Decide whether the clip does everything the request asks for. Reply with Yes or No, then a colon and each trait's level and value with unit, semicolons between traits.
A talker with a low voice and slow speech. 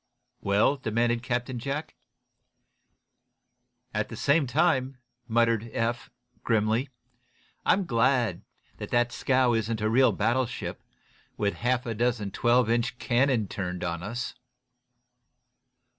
Yes: low, 120 Hz; slow, 115 wpm